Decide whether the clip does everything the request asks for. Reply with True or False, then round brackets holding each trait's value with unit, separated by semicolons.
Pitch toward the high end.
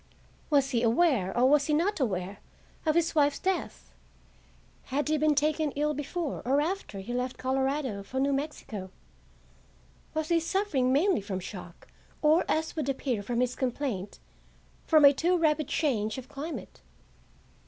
True (280 Hz)